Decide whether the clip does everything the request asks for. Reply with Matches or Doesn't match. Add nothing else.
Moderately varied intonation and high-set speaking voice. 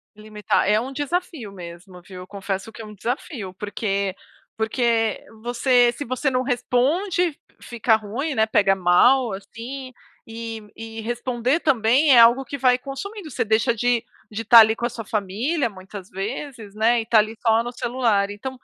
Matches